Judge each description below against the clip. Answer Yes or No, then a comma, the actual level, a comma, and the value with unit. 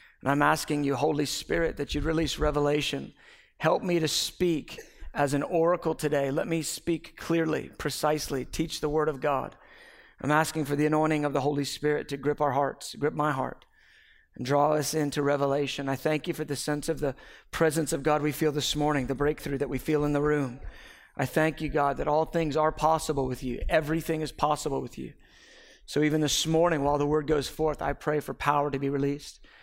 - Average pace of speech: No, fast, 210 wpm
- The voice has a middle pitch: Yes, medium, 150 Hz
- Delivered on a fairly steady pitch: Yes, narrow, 1.7 semitones